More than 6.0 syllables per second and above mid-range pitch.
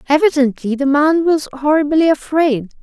No: 5.0 syllables/s; very high, 290 Hz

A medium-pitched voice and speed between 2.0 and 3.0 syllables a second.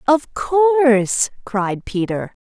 No: high, 245 Hz; 2.9 syllables/s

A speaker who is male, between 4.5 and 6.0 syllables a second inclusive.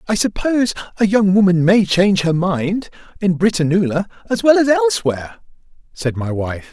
Yes: male; 5.3 syllables/s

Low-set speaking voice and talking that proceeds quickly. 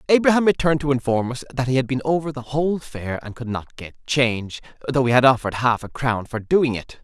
Yes: low, 130 Hz; fast, 240 wpm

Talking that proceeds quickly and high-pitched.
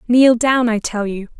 Yes: fast, 215 wpm; high, 230 Hz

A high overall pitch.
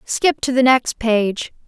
Yes: high, 245 Hz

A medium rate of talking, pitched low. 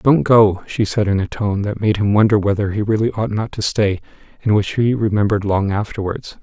No: fast, 225 wpm; low, 105 Hz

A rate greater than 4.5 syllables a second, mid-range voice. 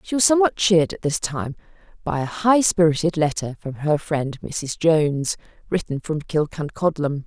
Yes: 5.2 syllables/s; medium, 165 Hz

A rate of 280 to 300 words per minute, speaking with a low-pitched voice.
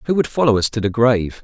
Yes: fast, 295 wpm; low, 120 Hz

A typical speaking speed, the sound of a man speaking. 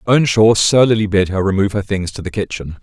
No: fast, 215 wpm; male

